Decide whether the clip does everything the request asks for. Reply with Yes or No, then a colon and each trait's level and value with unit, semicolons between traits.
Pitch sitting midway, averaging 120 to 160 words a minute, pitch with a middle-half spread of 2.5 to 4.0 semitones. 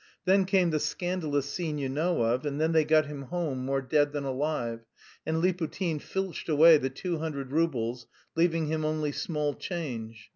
No: medium, 155 Hz; average, 180 wpm; average, 3.3 semitones